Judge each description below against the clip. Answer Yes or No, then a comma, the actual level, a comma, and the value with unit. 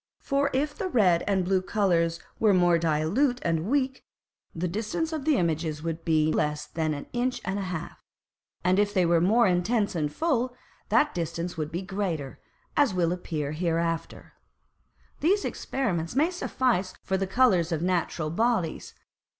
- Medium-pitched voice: Yes, medium, 180 Hz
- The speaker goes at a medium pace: Yes, average, 165 wpm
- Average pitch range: No, wide, 6.3 semitones